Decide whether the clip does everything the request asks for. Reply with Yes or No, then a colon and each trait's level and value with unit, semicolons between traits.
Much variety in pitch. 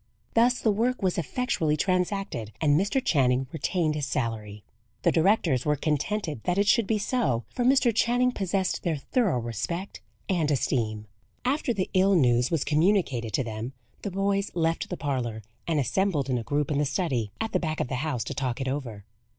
Yes: wide, 7.4 semitones